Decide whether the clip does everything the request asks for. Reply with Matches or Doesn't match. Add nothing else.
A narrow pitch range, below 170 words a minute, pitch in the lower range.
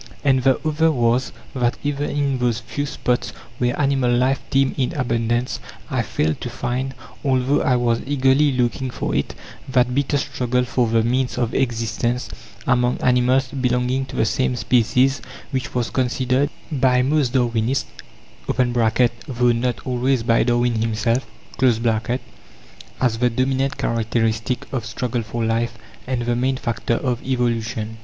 Matches